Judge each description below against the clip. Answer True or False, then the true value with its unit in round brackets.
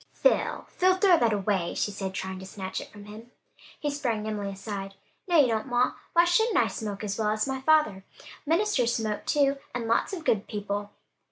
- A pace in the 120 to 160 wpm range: False (200 wpm)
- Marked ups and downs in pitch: True (6.2 semitones)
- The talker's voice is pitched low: False (220 Hz)